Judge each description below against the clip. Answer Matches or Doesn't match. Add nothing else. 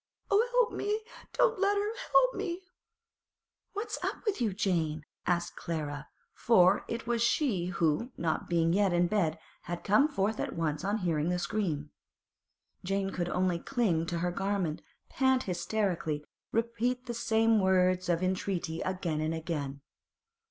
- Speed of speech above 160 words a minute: Doesn't match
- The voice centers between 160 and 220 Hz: Matches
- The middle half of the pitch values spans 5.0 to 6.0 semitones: Matches